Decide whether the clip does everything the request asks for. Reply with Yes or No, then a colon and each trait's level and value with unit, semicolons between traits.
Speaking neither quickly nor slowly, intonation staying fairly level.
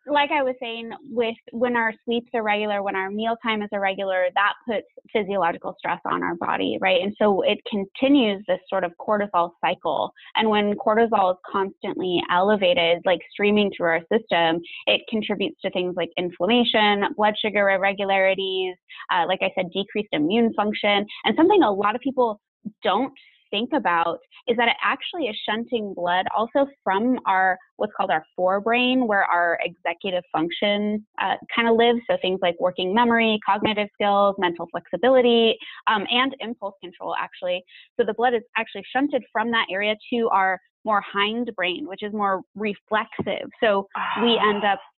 No: average, 170 wpm; average, 3.5 semitones